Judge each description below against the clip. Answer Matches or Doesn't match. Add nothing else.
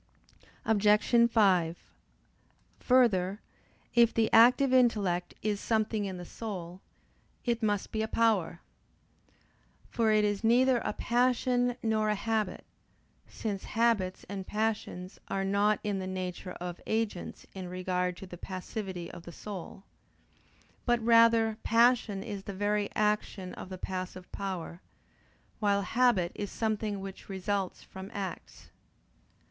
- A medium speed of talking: Doesn't match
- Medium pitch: Doesn't match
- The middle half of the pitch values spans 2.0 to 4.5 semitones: Matches